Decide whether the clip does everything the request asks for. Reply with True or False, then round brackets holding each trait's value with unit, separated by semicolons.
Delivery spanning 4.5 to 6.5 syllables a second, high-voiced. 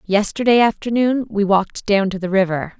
True (5.3 syllables/s; 205 Hz)